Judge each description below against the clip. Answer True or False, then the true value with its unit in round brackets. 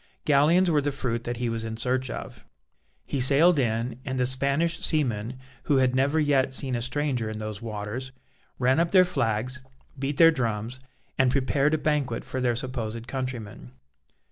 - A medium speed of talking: True (175 wpm)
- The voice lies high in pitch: False (130 Hz)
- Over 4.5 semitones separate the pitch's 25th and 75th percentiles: False (3.4 semitones)